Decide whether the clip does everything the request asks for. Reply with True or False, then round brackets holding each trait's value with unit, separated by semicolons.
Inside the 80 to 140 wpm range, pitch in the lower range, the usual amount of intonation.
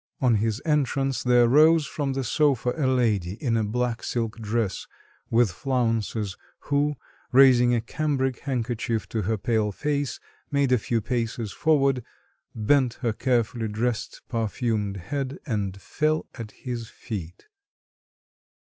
True (135 wpm; 120 Hz; 3.5 semitones)